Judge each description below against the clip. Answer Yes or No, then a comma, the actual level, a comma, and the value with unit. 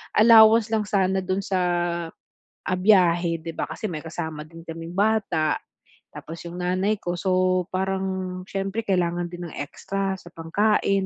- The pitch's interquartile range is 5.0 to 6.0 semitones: No, narrow, 2.5 semitones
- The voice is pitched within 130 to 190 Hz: Yes, medium, 185 Hz